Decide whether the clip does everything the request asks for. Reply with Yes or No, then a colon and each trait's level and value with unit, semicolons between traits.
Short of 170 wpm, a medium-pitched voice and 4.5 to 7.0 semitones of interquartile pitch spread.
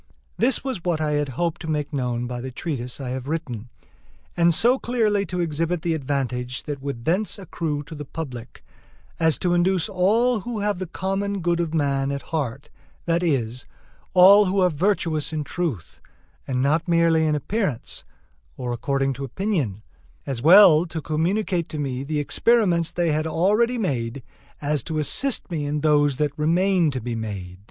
No: average, 180 wpm; medium, 155 Hz; average, 4.8 semitones